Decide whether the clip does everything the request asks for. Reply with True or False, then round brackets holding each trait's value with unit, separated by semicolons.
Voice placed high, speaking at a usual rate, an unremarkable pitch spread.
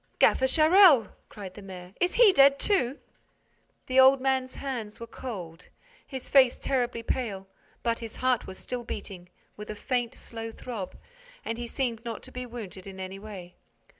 True (235 Hz; 170 wpm; 4.3 semitones)